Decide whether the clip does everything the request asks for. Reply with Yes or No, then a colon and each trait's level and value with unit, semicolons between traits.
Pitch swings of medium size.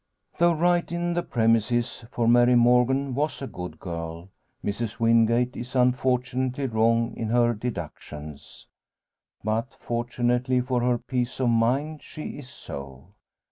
No: narrow, 2.2 semitones